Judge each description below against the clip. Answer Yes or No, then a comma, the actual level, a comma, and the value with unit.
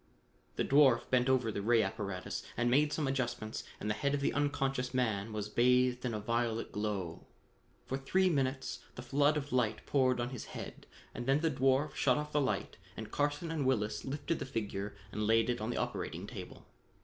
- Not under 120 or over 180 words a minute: No, average, 200 wpm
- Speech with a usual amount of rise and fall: Yes, average, 4.0 semitones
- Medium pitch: No, low, 125 Hz